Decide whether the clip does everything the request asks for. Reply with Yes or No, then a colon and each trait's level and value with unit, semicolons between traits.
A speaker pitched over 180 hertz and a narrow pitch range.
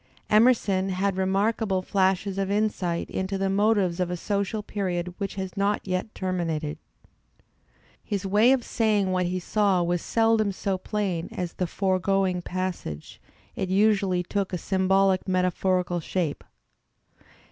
Yes: high, 190 Hz; narrow, 1.8 semitones